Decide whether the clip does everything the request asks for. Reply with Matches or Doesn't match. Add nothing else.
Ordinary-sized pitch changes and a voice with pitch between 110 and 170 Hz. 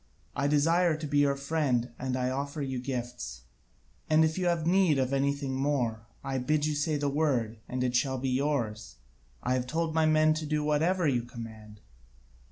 Matches